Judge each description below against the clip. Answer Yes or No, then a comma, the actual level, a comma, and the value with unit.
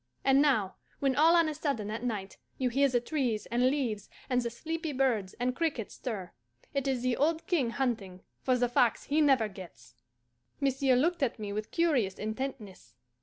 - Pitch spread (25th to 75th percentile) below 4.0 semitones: No, average, 4.4 semitones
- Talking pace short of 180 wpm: No, average, 185 wpm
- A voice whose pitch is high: Yes, very high, 250 Hz